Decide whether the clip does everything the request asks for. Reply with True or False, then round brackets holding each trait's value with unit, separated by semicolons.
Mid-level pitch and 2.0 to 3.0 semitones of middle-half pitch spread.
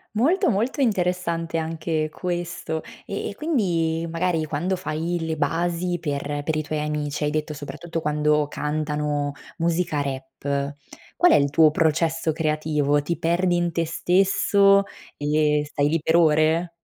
True (160 Hz; 2.6 semitones)